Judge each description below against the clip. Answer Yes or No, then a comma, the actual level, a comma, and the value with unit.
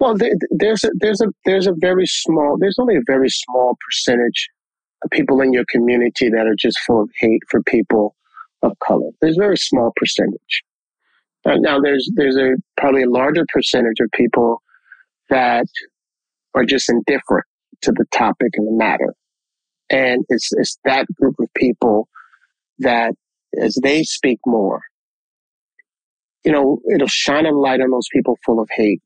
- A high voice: No, low, 135 Hz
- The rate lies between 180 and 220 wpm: No, average, 165 wpm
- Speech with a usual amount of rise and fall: No, wide, 8.1 semitones